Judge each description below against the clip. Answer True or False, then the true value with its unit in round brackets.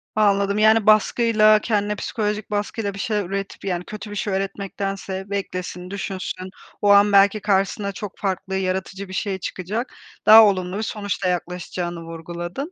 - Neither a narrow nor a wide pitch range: False (1.9 semitones)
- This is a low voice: False (200 Hz)